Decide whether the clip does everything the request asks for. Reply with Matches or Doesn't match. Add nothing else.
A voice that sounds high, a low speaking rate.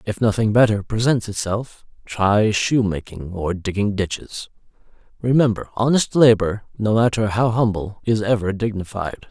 Doesn't match